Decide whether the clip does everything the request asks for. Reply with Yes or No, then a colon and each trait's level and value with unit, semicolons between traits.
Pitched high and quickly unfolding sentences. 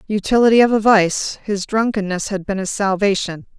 No: high, 205 Hz; average, 165 wpm